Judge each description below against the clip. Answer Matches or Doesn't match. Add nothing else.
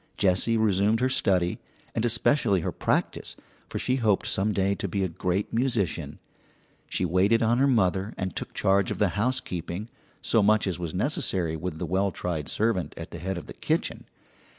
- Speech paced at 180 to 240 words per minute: Matches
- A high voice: Doesn't match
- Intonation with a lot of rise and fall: Doesn't match